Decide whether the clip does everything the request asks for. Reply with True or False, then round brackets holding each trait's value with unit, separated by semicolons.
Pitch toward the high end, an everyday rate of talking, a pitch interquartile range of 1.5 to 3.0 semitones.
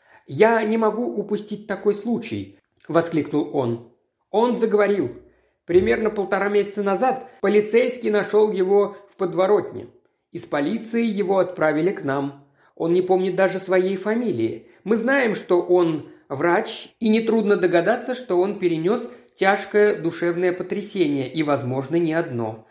False (195 Hz; 130 wpm; 4.1 semitones)